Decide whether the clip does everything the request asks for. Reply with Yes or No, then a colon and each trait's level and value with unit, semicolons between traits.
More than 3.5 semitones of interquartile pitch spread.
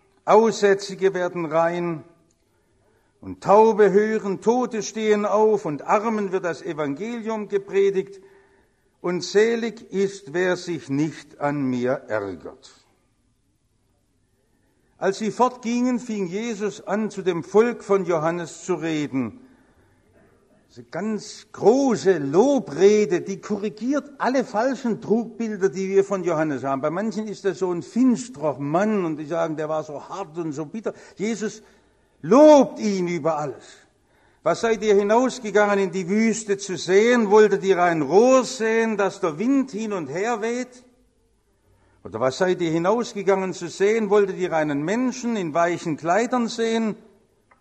Yes: average, 4.6 semitones